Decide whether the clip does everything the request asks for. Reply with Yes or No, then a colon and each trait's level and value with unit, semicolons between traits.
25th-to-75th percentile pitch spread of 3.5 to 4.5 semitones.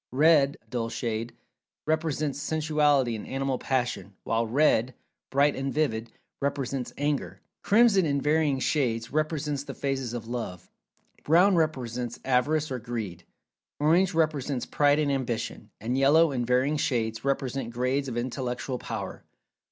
Yes: average, 3.8 semitones